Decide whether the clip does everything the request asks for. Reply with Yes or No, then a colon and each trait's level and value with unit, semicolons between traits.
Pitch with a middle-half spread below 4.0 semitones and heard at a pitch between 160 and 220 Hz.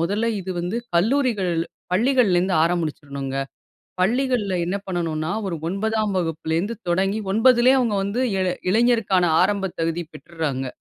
No: average, 4.5 semitones; high, 190 Hz